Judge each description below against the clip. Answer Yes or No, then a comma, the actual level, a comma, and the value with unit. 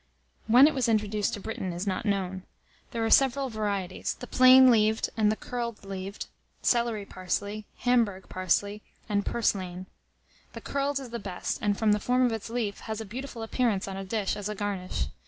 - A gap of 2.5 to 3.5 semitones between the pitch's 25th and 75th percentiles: Yes, average, 3.2 semitones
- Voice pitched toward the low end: No, high, 215 Hz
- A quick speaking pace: No, average, 190 wpm